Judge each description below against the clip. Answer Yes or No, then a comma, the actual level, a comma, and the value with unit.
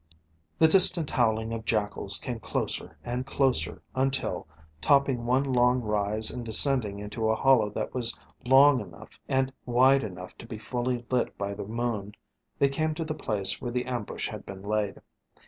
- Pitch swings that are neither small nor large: Yes, average, 3.8 semitones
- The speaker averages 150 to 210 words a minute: Yes, average, 170 wpm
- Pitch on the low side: Yes, low, 120 Hz